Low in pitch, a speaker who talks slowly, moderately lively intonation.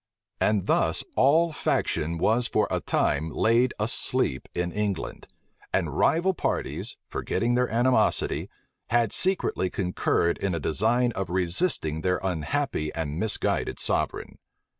No: low, 105 Hz; slow, 125 wpm; wide, 6.4 semitones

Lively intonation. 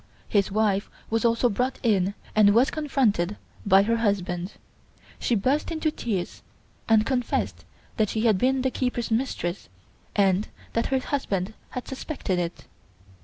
No: average, 4.3 semitones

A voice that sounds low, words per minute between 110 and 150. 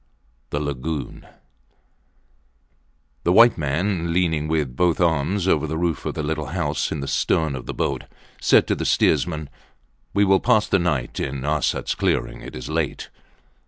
No: very low, 80 Hz; average, 160 wpm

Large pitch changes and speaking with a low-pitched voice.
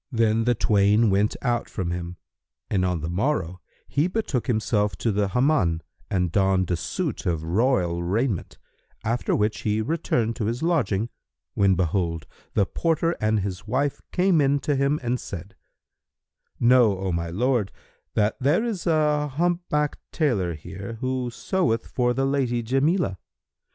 Yes: wide, 6.2 semitones; low, 115 Hz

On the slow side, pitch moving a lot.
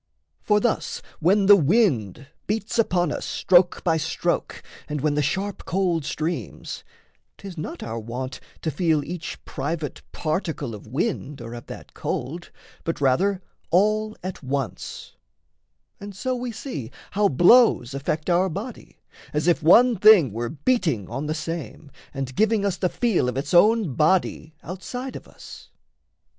No: average, 150 wpm; wide, 6.1 semitones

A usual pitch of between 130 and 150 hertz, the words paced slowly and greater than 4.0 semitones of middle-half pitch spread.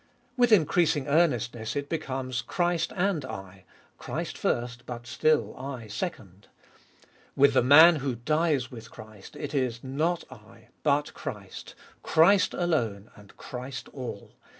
Yes: low, 135 Hz; slow, 130 wpm; average, 5.0 semitones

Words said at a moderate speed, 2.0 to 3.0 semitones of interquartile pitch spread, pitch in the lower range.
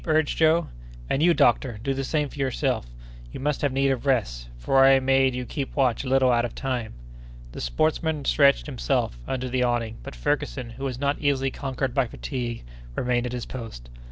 Yes: average, 195 wpm; narrow, 2.5 semitones; low, 130 Hz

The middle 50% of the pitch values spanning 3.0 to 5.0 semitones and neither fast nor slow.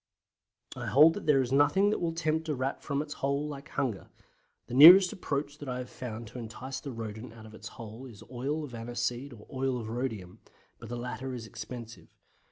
No: average, 3.8 semitones; fast, 210 wpm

